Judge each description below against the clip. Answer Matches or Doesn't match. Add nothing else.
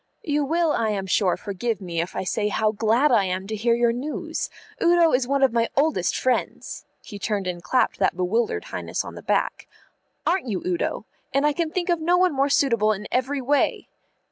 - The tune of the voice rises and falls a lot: Matches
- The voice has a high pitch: Matches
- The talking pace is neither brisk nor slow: Doesn't match